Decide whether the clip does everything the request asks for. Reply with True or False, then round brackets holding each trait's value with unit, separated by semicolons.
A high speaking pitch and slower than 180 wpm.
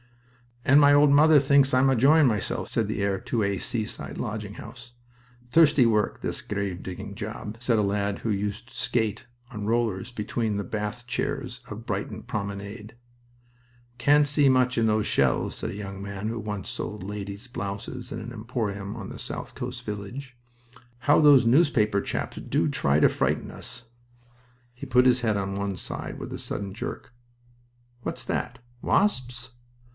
False (110 Hz; 170 wpm)